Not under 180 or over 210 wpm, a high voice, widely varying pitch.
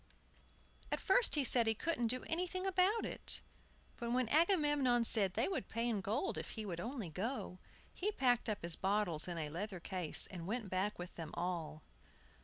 Yes: average, 190 wpm; high, 225 Hz; wide, 7.2 semitones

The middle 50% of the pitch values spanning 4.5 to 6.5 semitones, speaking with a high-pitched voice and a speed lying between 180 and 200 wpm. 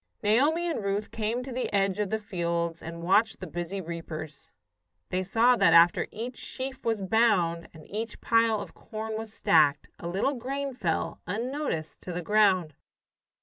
No: average, 5.2 semitones; high, 205 Hz; average, 170 wpm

